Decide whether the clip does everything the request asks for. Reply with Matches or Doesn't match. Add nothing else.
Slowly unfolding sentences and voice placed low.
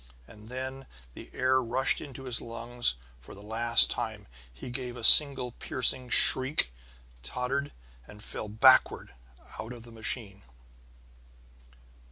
Matches